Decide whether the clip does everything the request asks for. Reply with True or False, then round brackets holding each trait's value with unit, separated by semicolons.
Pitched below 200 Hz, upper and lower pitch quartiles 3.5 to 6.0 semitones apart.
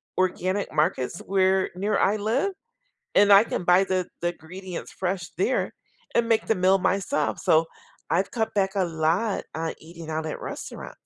False (185 Hz; 3.0 semitones)